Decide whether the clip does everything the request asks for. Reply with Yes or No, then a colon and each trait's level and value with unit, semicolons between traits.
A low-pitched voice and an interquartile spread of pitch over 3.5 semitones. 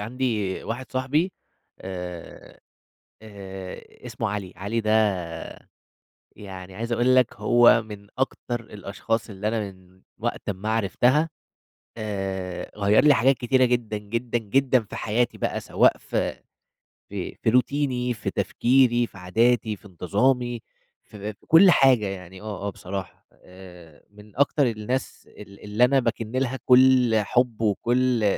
Yes: low, 110 Hz; average, 3.9 semitones